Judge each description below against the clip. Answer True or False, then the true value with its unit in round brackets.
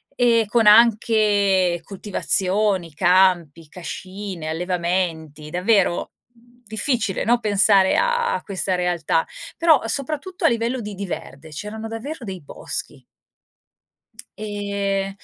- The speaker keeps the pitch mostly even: False (3.9 semitones)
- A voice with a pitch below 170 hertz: False (200 Hz)